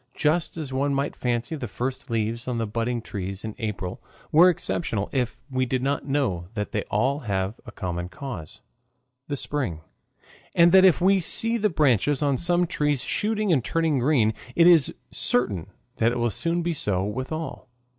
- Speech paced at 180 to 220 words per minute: Yes, average, 185 wpm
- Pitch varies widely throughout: Yes, wide, 6.2 semitones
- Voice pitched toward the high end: No, low, 130 Hz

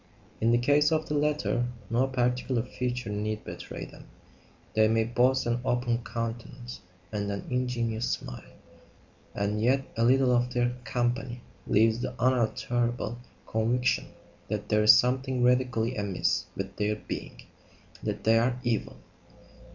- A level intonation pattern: Yes, narrow, 2.2 semitones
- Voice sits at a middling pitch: No, low, 120 Hz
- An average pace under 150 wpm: Yes, average, 140 wpm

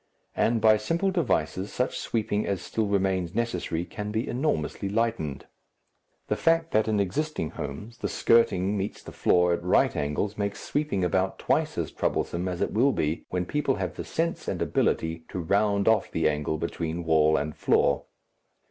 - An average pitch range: Yes, average, 5.0 semitones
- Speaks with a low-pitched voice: Yes, low, 100 Hz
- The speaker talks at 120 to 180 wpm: Yes, average, 175 wpm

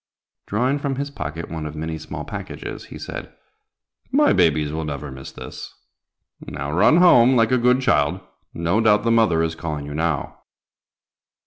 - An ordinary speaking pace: Yes, average, 165 wpm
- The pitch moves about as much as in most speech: No, wide, 7.7 semitones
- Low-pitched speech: Yes, very low, 85 Hz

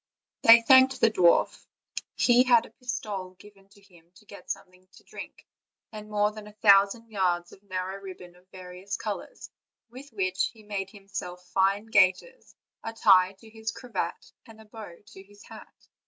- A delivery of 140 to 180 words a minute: Yes, average, 175 wpm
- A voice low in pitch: No, high, 200 Hz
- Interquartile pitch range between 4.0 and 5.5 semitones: No, average, 3.0 semitones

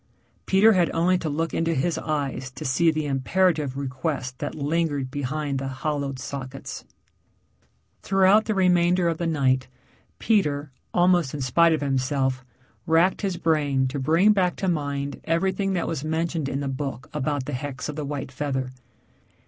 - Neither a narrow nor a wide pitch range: Yes, average, 3.9 semitones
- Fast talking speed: No, average, 165 wpm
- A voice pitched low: No, medium, 150 Hz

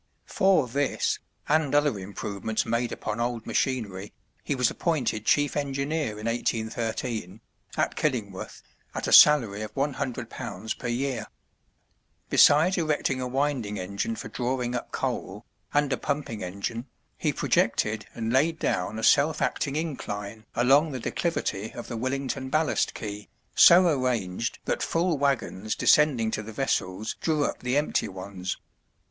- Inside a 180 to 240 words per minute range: No, average, 140 wpm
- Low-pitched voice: Yes, low, 125 Hz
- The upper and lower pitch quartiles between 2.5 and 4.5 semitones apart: No, average, 5.0 semitones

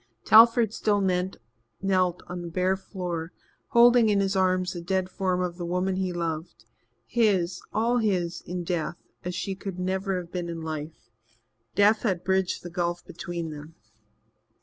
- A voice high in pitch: No, medium, 180 Hz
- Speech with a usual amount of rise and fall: No, narrow, 2.0 semitones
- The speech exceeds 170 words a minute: No, average, 160 wpm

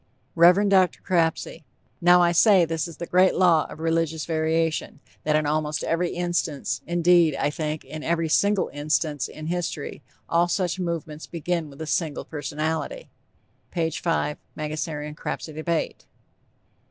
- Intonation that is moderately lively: No, narrow, 2.1 semitones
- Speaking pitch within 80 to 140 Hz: No, medium, 165 Hz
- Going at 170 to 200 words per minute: No, average, 145 wpm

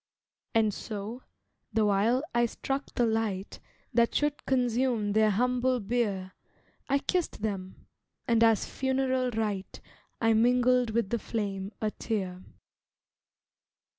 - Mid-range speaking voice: No, high, 225 Hz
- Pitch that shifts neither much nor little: Yes, average, 3.3 semitones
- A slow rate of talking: Yes, slow, 120 wpm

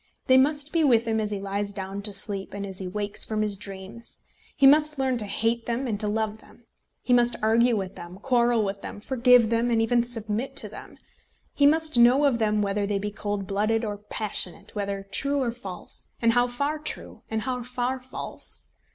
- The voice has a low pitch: No, high, 225 Hz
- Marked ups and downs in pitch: No, average, 3.4 semitones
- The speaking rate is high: Yes, fast, 210 wpm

